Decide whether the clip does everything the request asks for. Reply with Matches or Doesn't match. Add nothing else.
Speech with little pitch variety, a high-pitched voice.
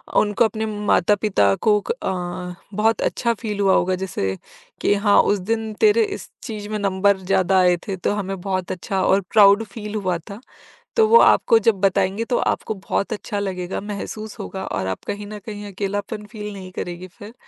Matches